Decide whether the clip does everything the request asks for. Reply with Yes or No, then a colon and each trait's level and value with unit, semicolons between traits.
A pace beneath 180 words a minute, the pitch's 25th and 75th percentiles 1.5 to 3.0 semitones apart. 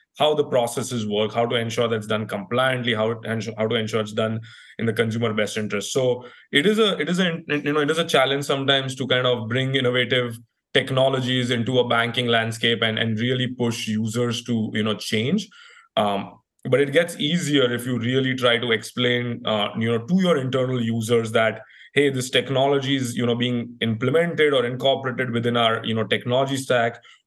No: average, 200 wpm; average, 2.7 semitones